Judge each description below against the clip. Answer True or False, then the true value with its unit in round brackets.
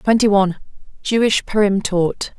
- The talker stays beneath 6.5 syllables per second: True (5.2 syllables/s)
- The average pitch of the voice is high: True (205 Hz)